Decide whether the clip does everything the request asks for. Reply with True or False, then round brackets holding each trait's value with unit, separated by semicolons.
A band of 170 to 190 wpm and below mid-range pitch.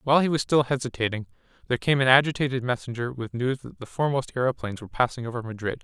False (205 wpm; 125 Hz)